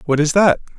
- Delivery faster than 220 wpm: Yes, fast, 230 wpm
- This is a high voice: No, medium, 160 Hz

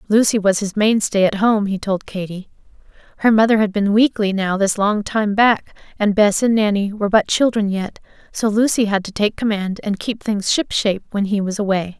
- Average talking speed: No, fast, 210 wpm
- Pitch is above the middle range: Yes, high, 205 Hz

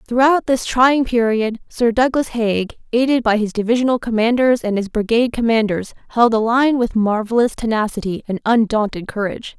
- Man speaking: No, female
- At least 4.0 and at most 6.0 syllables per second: Yes, 5.2 syllables/s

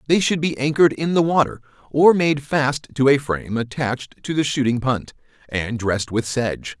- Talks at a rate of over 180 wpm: Yes, average, 195 wpm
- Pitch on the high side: No, low, 135 Hz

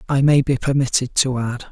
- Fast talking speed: Yes, fast, 210 wpm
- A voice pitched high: No, low, 130 Hz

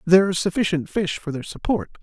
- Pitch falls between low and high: Yes, medium, 175 Hz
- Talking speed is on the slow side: No, fast, 205 wpm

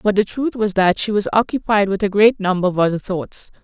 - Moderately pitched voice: No, high, 200 Hz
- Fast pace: Yes, fast, 245 wpm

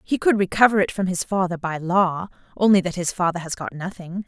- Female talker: Yes, female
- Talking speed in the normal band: No, fast, 225 wpm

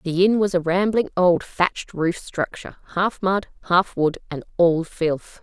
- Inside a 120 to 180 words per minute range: Yes, average, 175 wpm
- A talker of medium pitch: Yes, medium, 180 Hz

